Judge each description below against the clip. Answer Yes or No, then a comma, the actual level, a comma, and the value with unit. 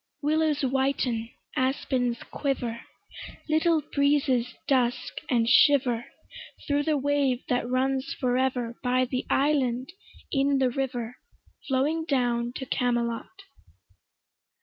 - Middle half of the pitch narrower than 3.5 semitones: Yes, narrow, 2.5 semitones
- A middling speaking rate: No, slow, 105 wpm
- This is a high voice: Yes, very high, 260 Hz